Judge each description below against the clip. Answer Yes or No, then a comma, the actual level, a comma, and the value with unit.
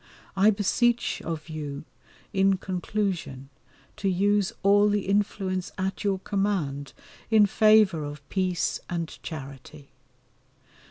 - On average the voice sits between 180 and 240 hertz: Yes, high, 190 Hz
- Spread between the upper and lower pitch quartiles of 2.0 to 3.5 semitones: No, average, 4.7 semitones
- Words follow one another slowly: Yes, slow, 110 wpm